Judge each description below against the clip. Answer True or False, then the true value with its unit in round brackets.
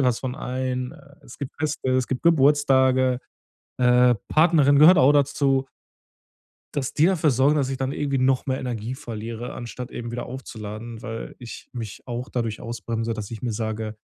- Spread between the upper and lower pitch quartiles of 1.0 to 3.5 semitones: True (2.7 semitones)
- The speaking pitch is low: True (130 Hz)